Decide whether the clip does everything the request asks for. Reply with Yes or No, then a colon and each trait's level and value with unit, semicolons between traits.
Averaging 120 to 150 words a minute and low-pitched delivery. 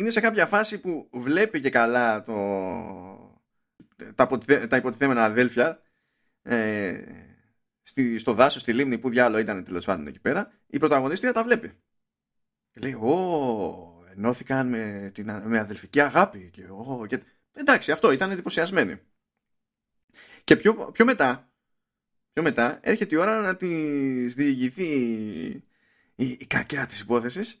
Yes: average, 125 wpm; low, 130 Hz